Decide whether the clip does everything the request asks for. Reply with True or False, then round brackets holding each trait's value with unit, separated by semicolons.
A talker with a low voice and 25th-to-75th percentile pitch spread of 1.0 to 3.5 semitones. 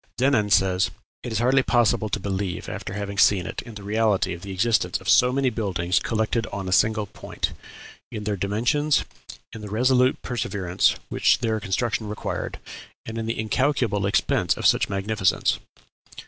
True (105 Hz; 3.2 semitones)